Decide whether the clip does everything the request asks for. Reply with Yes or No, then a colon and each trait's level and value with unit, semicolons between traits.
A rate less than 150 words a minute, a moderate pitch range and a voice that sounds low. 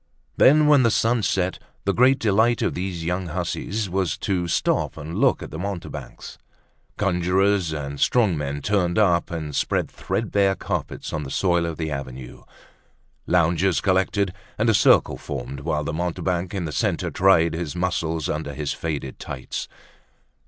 No: average, 160 wpm; average, 3.8 semitones; very low, 90 Hz